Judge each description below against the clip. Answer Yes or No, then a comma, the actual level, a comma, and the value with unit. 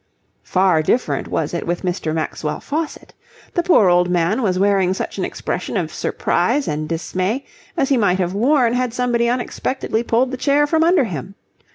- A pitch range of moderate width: No, wide, 6.4 semitones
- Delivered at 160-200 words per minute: Yes, average, 180 wpm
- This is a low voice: No, high, 205 Hz